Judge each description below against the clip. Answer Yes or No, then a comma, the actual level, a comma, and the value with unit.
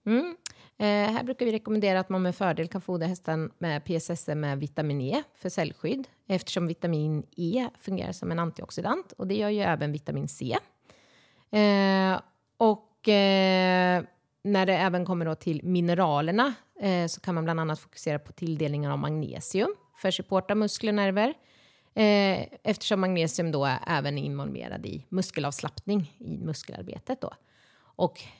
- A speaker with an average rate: Yes, average, 160 wpm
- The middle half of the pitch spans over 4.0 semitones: Yes, average, 4.4 semitones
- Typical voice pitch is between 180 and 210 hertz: Yes, medium, 185 Hz